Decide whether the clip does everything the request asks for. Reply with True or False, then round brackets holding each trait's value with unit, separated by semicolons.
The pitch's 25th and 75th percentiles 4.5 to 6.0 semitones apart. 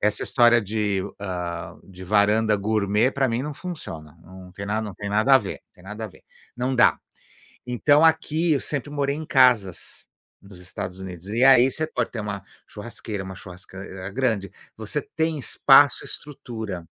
True (5.3 semitones)